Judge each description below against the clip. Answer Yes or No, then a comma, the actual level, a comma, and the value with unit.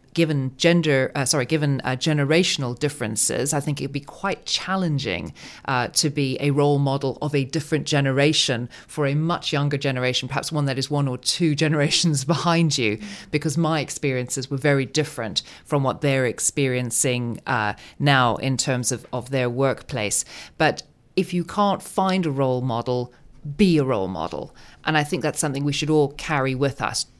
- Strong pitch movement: No, average, 3.1 semitones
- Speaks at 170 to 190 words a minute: Yes, average, 180 wpm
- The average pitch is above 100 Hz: Yes, medium, 140 Hz